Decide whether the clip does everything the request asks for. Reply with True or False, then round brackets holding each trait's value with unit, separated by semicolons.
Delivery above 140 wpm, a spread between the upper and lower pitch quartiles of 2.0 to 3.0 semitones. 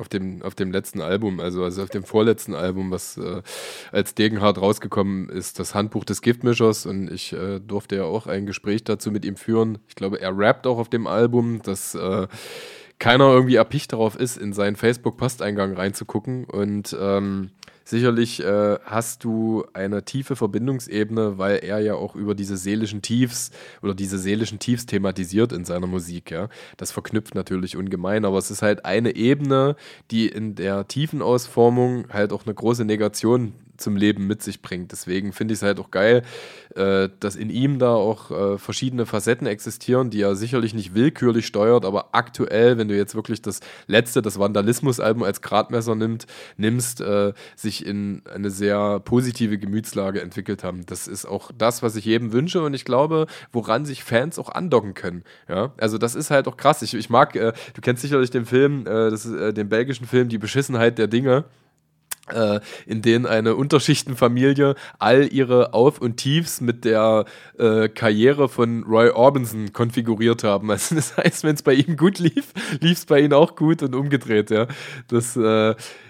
False (180 wpm; 3.4 semitones)